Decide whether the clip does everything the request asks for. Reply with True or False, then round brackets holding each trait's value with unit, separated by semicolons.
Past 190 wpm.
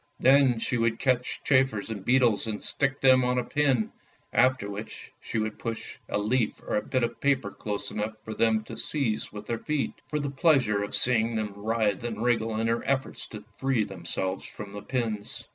True (200 wpm)